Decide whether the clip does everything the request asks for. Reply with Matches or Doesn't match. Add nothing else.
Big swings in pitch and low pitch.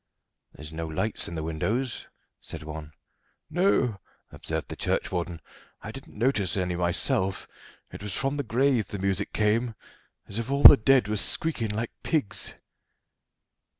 Matches